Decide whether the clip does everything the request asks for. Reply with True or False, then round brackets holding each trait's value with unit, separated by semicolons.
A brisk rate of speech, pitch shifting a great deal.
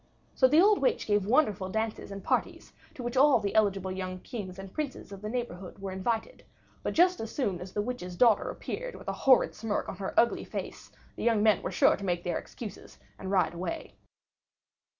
False (210 wpm; 4.8 semitones)